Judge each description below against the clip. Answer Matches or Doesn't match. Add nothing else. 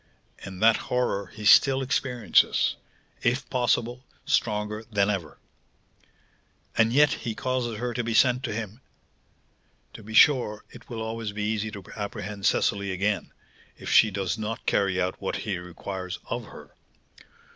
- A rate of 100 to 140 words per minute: Doesn't match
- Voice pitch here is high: Doesn't match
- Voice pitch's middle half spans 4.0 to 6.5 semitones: Doesn't match